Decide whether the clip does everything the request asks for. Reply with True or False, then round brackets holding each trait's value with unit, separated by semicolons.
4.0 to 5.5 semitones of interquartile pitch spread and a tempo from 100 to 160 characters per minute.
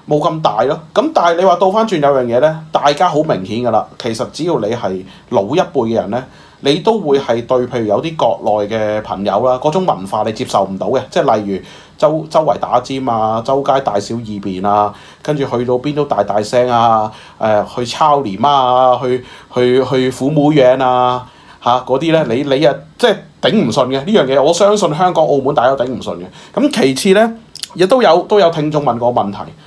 False (5.1 semitones; 295 characters per minute)